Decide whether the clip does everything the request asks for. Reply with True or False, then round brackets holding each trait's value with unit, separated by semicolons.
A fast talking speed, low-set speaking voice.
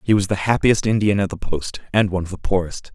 True (265 wpm; 95 Hz)